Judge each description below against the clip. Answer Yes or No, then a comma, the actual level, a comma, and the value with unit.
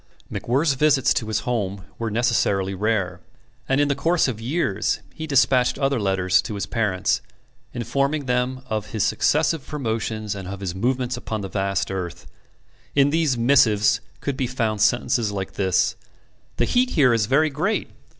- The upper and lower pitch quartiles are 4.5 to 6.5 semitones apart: Yes, average, 5.2 semitones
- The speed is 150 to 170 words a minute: Yes, average, 165 wpm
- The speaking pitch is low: Yes, low, 120 Hz